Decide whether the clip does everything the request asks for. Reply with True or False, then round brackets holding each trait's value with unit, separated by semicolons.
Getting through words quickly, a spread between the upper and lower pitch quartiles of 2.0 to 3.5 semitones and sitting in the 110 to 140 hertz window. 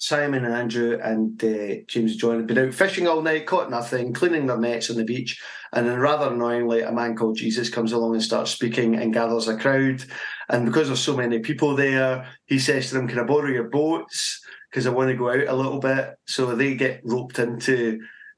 True (225 wpm; 2.8 semitones; 125 Hz)